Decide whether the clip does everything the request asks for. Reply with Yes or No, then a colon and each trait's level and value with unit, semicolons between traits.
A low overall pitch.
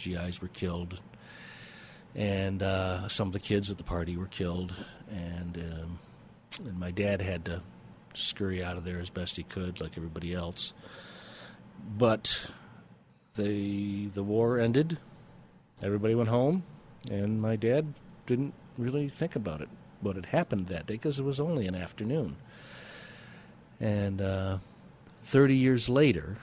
Yes: low, 100 Hz